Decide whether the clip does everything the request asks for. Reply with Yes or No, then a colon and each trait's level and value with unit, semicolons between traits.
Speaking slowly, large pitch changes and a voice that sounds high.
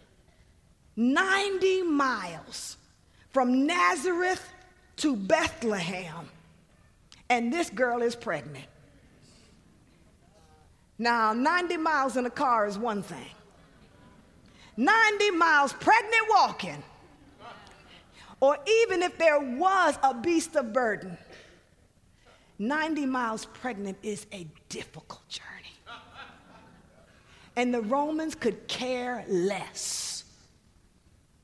Yes: slow, 90 wpm; wide, 8.5 semitones; very high, 255 Hz